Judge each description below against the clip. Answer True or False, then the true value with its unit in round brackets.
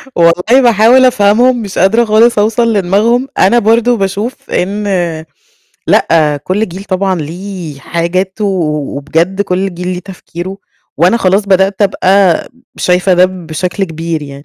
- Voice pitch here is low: False (190 Hz)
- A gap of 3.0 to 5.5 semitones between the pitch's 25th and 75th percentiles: True (3.4 semitones)